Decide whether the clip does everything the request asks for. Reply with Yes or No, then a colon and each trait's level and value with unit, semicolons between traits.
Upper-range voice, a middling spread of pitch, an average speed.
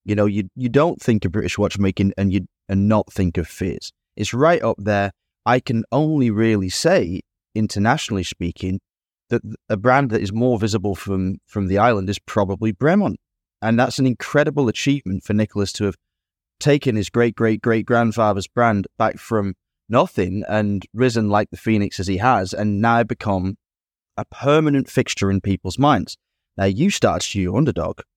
No: low, 105 Hz; average, 3.7 semitones; average, 180 wpm